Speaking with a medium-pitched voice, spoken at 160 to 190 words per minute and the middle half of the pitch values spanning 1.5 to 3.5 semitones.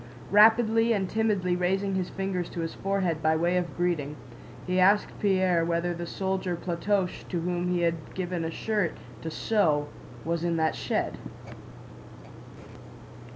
No: medium, 180 Hz; average, 150 wpm; narrow, 2.5 semitones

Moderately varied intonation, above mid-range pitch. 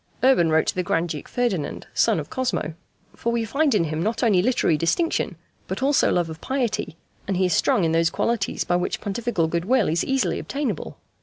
No: wide, 6.8 semitones; high, 195 Hz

